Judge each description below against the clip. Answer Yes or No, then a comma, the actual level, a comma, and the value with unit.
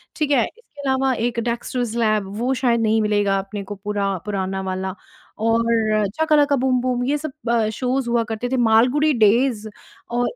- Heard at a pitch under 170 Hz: No, high, 235 Hz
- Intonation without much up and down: No, average, 3.3 semitones